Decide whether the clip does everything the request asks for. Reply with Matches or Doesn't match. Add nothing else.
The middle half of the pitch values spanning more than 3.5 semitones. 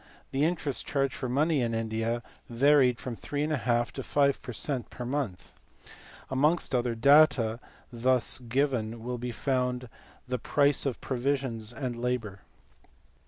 Doesn't match